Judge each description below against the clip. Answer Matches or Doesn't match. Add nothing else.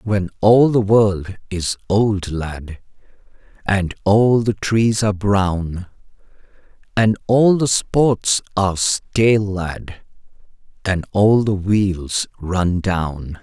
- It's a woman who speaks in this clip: Doesn't match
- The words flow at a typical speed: Doesn't match